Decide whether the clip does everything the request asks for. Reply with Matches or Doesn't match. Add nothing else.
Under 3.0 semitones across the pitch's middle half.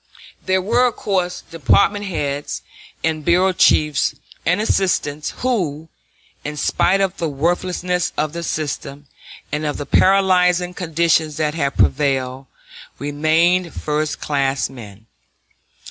Doesn't match